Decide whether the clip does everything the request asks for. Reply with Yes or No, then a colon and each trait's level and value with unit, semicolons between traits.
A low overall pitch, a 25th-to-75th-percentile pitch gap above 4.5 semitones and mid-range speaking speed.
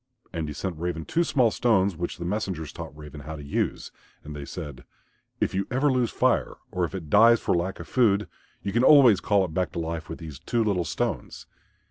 No: very low, 90 Hz; wide, 5.4 semitones; fast, 220 wpm